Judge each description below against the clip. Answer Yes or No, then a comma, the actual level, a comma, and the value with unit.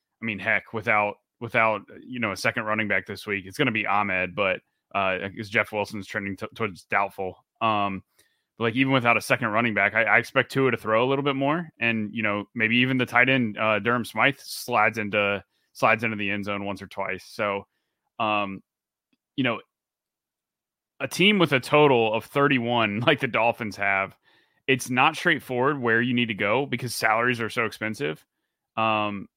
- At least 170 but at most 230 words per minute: Yes, average, 200 wpm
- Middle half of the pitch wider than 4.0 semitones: No, average, 3.1 semitones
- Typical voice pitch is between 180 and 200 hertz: No, low, 110 Hz